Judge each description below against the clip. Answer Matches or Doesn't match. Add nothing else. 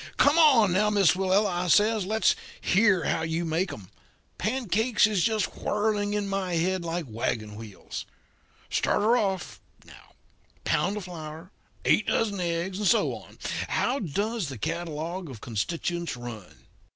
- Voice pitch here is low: Doesn't match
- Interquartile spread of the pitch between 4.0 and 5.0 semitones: Matches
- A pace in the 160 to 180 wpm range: Doesn't match